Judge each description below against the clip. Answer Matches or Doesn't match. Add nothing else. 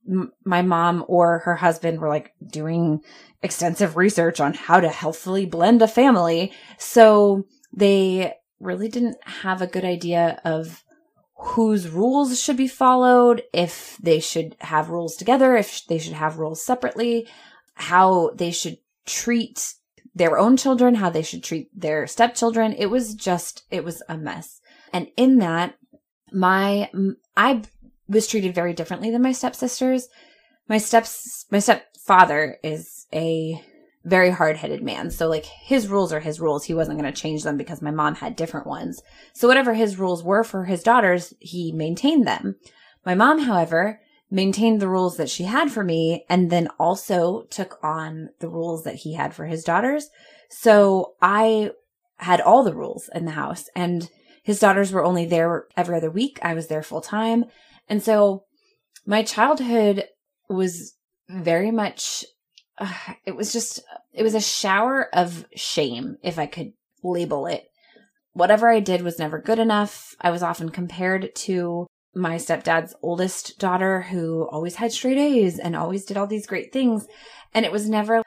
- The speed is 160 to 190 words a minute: Matches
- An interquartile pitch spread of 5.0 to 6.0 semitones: Matches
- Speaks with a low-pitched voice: Doesn't match